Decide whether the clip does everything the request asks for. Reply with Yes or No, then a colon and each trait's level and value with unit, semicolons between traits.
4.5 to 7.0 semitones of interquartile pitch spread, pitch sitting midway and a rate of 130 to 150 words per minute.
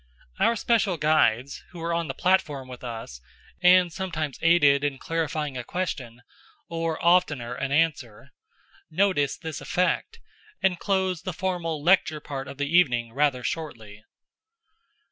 Yes: average, 4.9 semitones; medium, 155 Hz; average, 140 wpm